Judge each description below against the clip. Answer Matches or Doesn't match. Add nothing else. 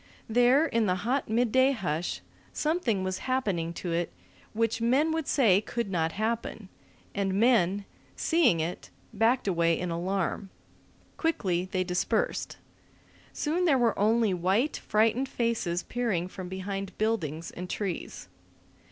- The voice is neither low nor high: Doesn't match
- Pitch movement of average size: Matches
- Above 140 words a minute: Doesn't match